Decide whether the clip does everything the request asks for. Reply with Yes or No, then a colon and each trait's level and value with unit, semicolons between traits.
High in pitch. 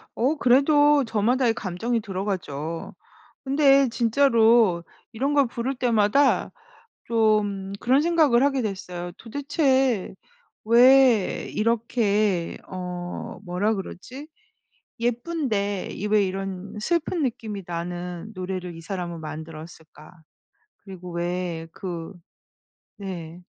Yes: high, 210 Hz